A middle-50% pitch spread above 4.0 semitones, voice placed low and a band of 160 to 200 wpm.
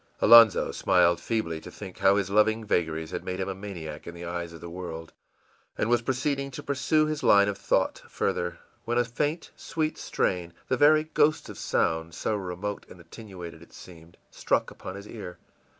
Yes: wide, 5.4 semitones; low, 100 Hz; average, 190 wpm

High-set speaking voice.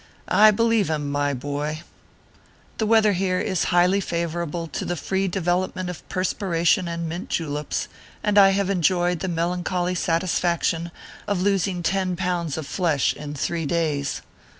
No: medium, 175 Hz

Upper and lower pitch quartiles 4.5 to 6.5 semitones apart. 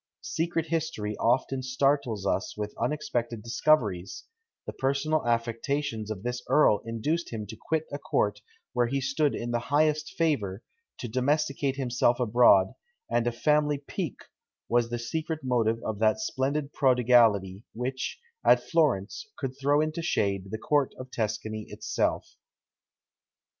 Yes: average, 4.8 semitones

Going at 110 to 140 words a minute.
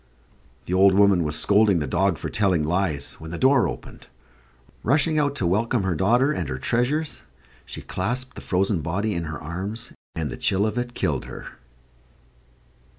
No: average, 175 wpm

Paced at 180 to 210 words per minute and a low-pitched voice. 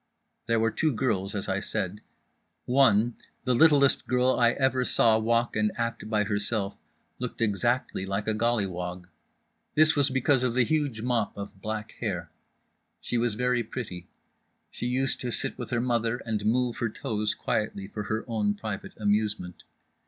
No: average, 165 wpm; low, 115 Hz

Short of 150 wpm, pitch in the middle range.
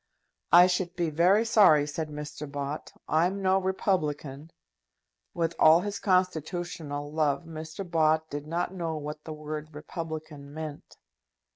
Yes: slow, 135 wpm; medium, 160 Hz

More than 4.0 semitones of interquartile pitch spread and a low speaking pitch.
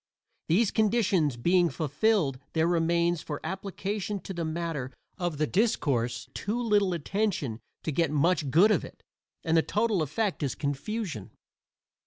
No: wide, 5.5 semitones; medium, 170 Hz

